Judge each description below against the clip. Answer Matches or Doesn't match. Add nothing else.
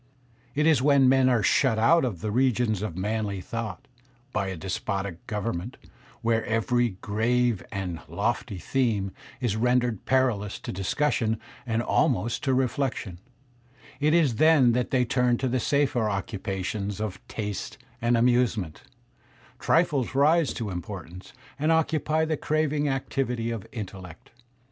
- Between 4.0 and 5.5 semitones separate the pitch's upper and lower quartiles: Matches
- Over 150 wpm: Doesn't match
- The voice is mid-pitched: Doesn't match